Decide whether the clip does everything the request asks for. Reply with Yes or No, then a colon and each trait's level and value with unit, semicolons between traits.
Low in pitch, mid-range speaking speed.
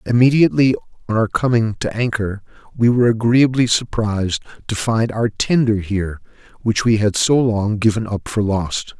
Yes: low, 110 Hz; average, 160 wpm